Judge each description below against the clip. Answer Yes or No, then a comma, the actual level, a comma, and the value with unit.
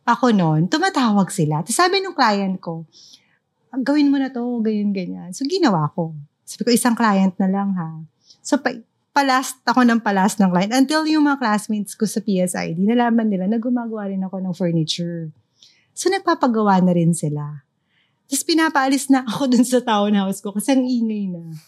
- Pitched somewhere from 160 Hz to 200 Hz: No, high, 210 Hz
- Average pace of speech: No, fast, 175 wpm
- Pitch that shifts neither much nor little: No, wide, 6.5 semitones